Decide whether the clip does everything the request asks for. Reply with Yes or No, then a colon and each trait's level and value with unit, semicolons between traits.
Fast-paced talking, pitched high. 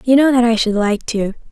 Yes: fast, 280 wpm; high, 235 Hz